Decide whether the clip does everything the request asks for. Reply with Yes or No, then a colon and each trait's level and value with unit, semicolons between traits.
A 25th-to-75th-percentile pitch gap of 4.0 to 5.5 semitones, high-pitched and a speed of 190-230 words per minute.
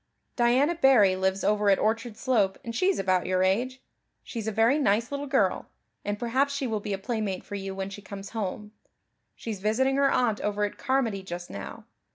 Yes: average, 4.7 semitones; high, 215 Hz; average, 200 wpm